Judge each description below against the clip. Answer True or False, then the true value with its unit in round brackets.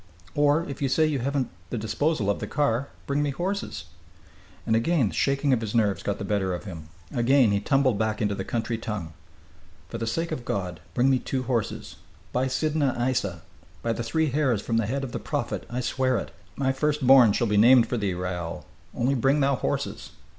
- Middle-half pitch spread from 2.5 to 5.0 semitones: True (4.5 semitones)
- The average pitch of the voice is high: False (125 Hz)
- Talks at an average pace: False (210 wpm)